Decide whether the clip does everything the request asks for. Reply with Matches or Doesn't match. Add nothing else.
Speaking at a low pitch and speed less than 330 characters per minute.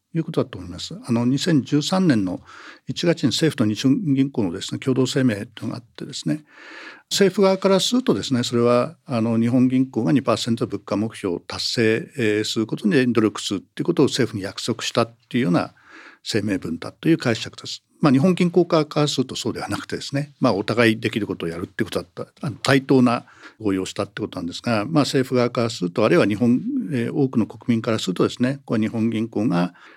Doesn't match